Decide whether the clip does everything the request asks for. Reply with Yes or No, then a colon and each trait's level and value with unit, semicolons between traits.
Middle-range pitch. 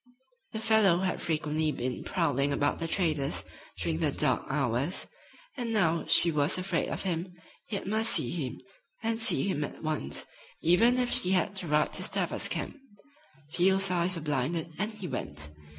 Yes: medium, 175 Hz